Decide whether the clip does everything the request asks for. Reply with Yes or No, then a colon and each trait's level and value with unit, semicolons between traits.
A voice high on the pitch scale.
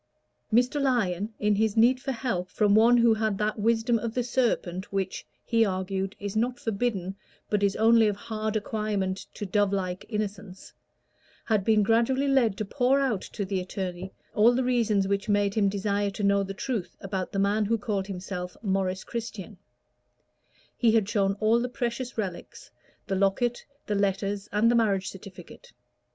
Yes: high, 210 Hz